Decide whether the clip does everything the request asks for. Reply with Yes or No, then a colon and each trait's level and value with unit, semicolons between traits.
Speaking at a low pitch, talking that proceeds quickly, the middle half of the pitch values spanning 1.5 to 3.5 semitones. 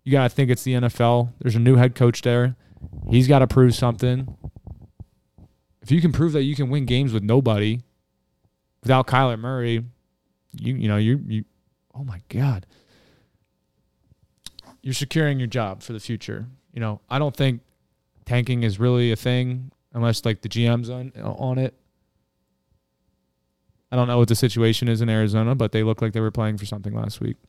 No: low, 120 Hz; average, 185 wpm; average, 2.8 semitones